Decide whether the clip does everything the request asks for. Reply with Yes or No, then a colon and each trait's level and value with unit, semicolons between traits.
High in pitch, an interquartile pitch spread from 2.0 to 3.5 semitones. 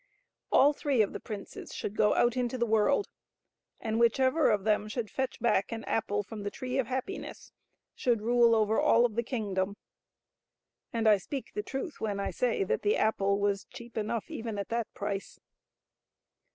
Yes: high, 225 Hz; average, 2.8 semitones